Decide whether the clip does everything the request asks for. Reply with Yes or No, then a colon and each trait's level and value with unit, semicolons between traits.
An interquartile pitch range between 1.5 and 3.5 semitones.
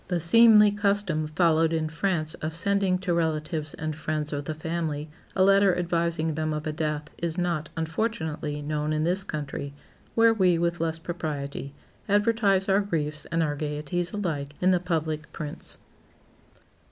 Yes: average, 3.1 semitones